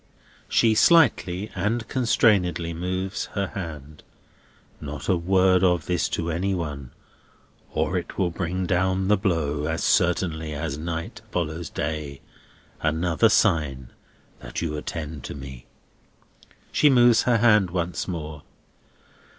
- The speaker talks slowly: Yes, slow, 125 wpm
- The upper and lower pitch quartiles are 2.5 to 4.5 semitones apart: Yes, average, 3.5 semitones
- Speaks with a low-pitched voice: Yes, very low, 85 Hz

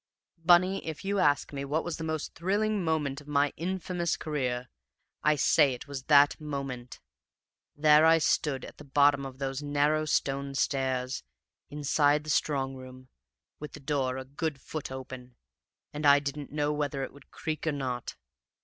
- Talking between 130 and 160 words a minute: No, average, 170 wpm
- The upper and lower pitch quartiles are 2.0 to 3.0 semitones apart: Yes, narrow, 2.4 semitones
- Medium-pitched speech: Yes, medium, 145 Hz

